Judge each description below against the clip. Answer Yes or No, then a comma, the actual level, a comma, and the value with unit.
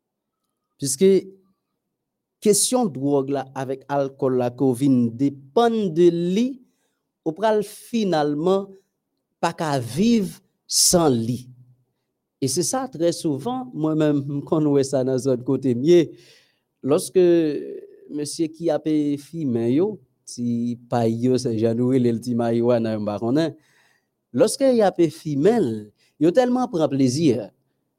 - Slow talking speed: Yes, slow, 110 wpm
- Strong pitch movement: Yes, wide, 6.9 semitones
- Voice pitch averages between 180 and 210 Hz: No, medium, 150 Hz